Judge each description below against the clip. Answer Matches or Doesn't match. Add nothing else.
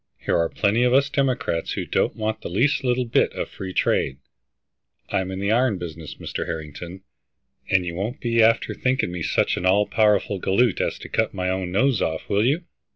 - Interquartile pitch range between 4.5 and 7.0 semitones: Matches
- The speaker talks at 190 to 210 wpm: Matches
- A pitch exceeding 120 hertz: Doesn't match